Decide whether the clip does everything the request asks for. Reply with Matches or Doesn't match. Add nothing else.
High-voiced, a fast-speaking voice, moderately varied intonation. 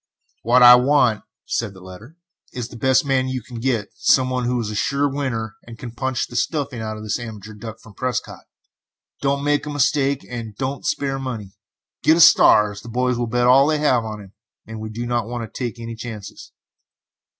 Doesn't match